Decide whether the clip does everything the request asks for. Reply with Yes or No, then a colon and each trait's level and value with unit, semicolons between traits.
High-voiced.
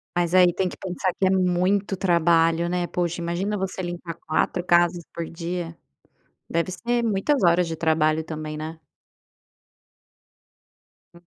No: medium, 175 Hz